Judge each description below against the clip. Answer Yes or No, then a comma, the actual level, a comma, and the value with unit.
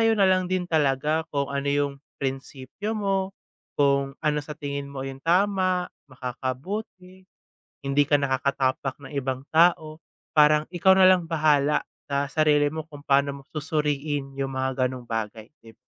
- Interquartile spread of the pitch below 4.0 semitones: Yes, average, 3.2 semitones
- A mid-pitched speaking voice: Yes, medium, 145 Hz